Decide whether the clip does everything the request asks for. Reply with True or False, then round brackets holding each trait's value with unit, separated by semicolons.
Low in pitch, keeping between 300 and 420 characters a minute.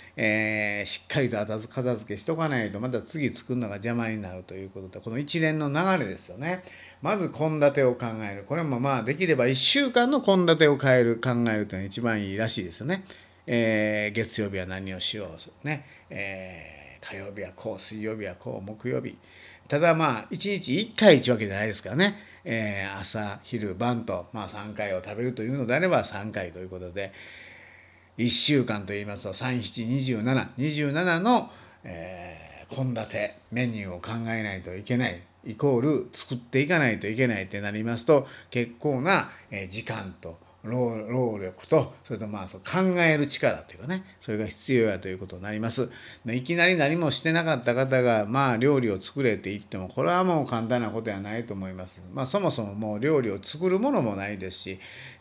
True (115 Hz; 350 characters per minute)